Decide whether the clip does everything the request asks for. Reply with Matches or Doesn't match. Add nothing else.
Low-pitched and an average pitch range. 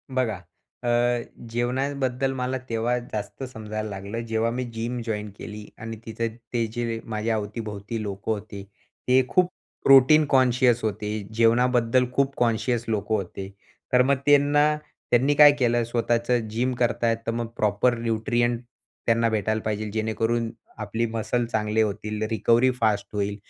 Doesn't match